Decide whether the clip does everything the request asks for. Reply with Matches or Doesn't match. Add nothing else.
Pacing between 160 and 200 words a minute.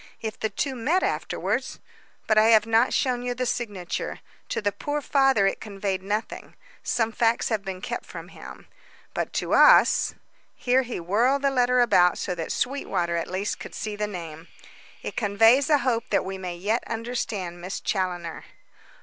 Matches